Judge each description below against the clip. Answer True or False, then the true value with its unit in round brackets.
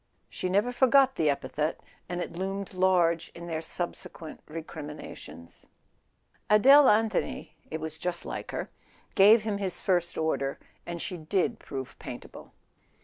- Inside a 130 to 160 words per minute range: True (135 wpm)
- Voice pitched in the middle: True (175 Hz)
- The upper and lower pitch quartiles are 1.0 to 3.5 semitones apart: False (4.2 semitones)